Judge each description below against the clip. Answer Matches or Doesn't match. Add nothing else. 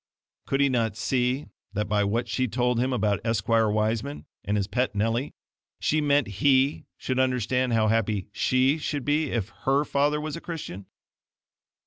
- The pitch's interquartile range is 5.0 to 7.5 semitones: Doesn't match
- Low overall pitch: Matches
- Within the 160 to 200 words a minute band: Matches